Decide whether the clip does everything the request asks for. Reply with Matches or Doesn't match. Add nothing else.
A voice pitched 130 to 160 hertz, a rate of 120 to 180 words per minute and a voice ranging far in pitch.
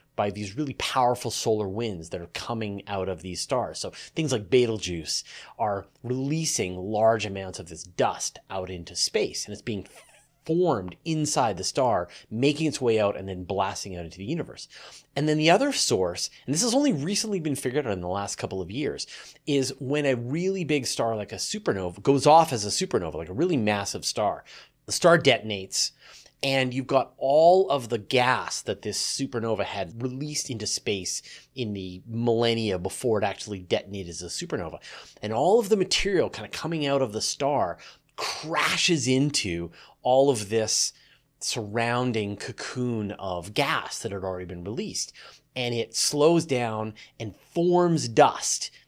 Doesn't match